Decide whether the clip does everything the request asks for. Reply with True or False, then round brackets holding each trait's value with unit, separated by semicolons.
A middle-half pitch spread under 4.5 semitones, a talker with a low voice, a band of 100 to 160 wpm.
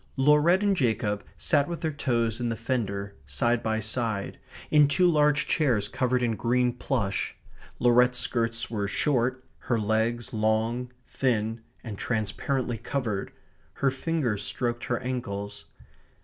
True (3.2 semitones; 120 Hz; 135 wpm)